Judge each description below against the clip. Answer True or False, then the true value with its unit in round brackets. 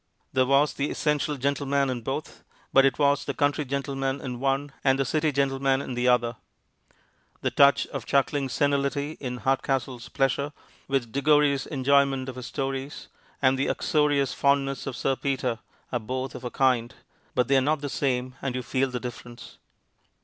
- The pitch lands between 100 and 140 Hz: True (135 Hz)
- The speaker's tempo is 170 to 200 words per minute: True (175 wpm)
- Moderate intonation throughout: False (1.6 semitones)